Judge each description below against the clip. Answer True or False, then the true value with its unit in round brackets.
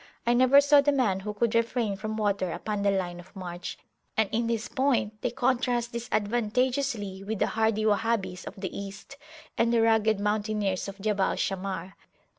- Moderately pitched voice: False (215 Hz)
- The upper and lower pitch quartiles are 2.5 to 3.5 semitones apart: True (3.2 semitones)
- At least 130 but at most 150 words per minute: False (175 wpm)